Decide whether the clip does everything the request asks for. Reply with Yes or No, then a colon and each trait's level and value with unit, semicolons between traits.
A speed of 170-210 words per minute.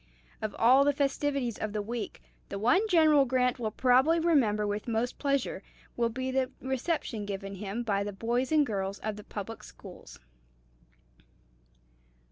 No: average, 155 wpm